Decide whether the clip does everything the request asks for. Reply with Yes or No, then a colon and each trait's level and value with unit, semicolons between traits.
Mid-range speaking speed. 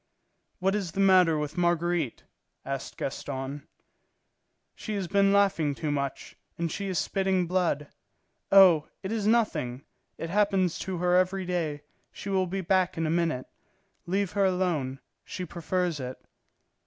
Yes: average, 150 wpm